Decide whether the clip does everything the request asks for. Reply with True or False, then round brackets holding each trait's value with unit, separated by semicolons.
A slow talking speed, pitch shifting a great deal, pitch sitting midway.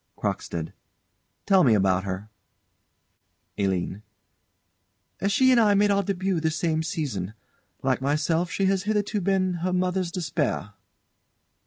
True (125 wpm; 7.3 semitones; 170 Hz)